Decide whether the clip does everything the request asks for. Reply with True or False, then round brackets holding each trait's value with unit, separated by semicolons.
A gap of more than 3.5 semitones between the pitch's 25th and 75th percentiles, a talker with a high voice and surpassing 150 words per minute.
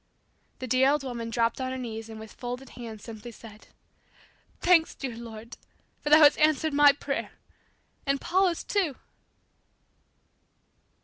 False (4.3 semitones; 255 Hz; 140 wpm)